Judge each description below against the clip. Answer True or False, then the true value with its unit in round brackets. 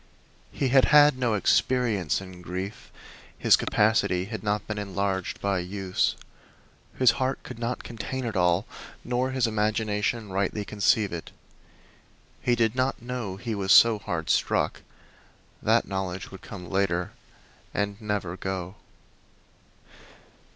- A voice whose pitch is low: True (105 Hz)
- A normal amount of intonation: True (3.6 semitones)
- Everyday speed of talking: False (130 wpm)